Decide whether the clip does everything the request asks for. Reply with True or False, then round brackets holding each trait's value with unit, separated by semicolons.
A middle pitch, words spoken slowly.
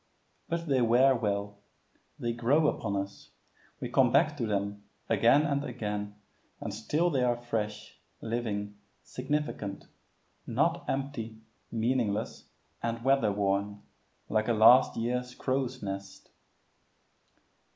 False (115 Hz; 120 wpm)